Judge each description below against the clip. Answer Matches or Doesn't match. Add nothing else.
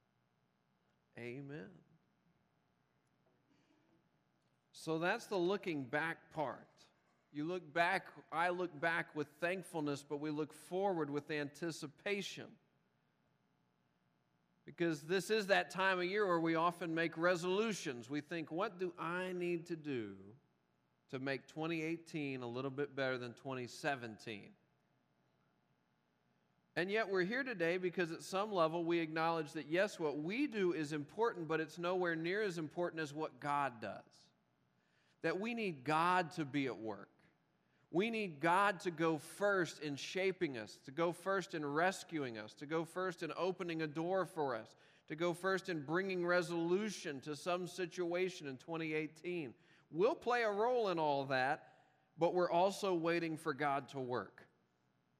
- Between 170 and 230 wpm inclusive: Doesn't match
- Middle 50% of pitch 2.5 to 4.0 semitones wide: Matches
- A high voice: Doesn't match